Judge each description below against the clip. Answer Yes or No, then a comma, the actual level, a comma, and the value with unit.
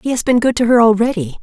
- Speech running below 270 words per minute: No, fast, 295 wpm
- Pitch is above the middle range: Yes, high, 230 Hz